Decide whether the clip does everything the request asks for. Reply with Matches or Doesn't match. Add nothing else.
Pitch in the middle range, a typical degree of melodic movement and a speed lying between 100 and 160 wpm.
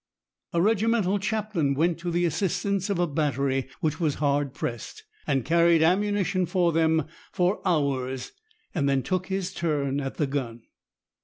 Matches